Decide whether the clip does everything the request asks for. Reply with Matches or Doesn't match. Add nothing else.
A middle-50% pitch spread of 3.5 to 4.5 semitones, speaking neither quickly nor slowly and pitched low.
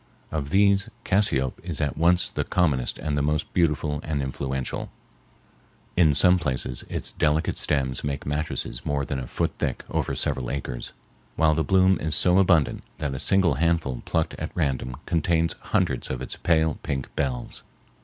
Matches